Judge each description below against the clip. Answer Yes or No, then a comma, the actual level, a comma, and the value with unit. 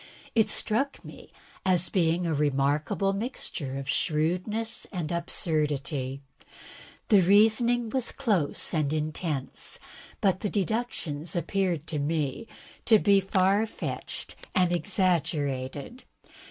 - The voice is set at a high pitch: No, medium, 175 Hz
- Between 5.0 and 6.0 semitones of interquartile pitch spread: Yes, wide, 5.4 semitones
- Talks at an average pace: No, slow, 110 wpm